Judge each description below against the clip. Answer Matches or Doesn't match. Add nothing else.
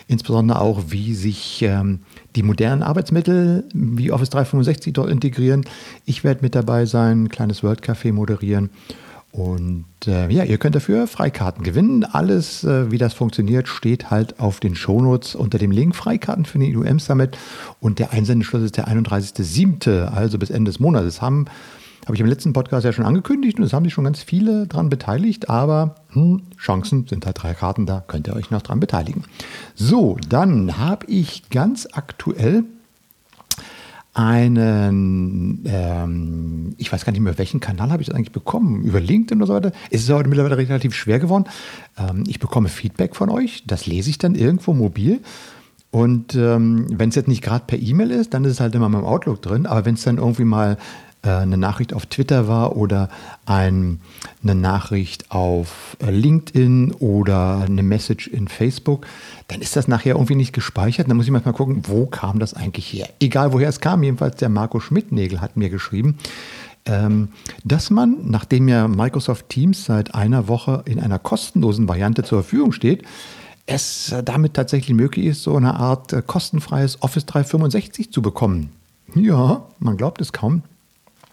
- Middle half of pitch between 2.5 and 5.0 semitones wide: Doesn't match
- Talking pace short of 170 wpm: Doesn't match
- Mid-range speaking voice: Doesn't match